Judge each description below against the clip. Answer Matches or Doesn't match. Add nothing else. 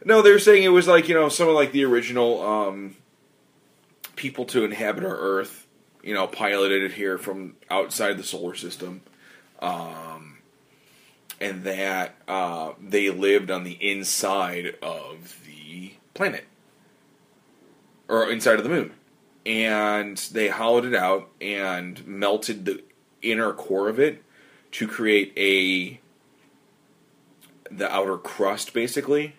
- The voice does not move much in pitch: Doesn't match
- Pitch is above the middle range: Doesn't match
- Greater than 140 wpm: Doesn't match